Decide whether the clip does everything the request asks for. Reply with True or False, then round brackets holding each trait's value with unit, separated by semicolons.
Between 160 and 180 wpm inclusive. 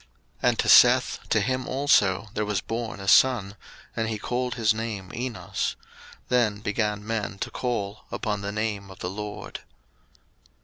True (165 wpm)